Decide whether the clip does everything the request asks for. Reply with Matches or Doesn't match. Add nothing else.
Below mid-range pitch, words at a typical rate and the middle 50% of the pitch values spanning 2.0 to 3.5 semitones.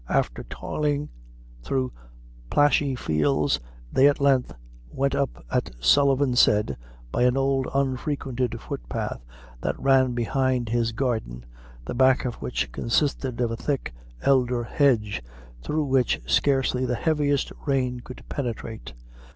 Doesn't match